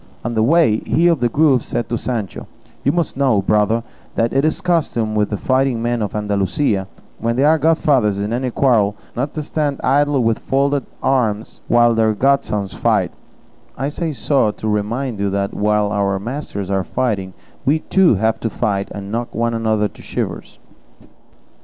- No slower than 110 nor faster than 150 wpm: No, average, 185 wpm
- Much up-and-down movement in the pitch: No, average, 4.7 semitones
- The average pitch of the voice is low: Yes, low, 115 Hz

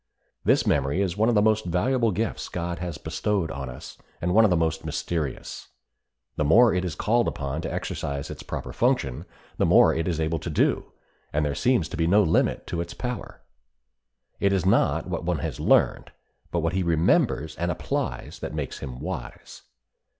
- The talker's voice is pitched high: No, very low, 85 Hz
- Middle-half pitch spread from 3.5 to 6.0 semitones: Yes, average, 3.9 semitones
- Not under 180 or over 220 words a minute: Yes, average, 195 wpm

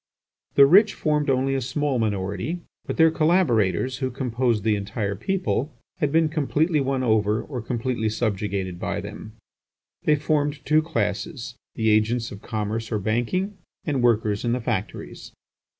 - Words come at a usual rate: Yes, average, 150 wpm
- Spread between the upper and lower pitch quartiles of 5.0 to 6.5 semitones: Yes, wide, 5.5 semitones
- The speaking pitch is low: Yes, low, 120 Hz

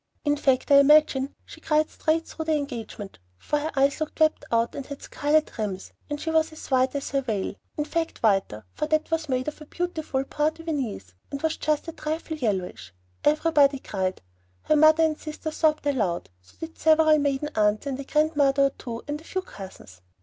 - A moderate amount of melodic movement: Yes, average, 3.4 semitones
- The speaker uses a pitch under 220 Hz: No, very high, 290 Hz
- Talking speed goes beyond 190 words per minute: Yes, average, 200 wpm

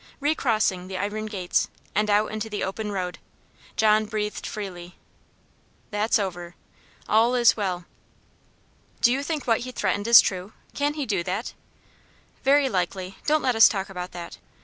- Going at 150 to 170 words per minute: Yes, average, 160 wpm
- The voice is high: Yes, high, 210 Hz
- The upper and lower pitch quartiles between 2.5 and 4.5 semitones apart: Yes, average, 3.8 semitones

